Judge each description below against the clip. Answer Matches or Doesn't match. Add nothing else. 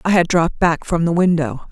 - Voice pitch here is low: Doesn't match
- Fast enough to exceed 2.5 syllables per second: Matches